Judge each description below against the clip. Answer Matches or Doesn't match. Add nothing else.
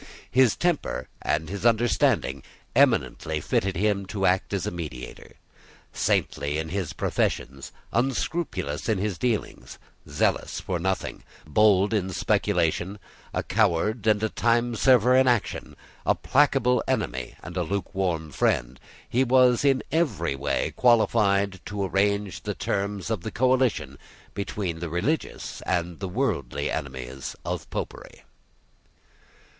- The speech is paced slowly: Matches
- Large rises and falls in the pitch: Matches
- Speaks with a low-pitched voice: Matches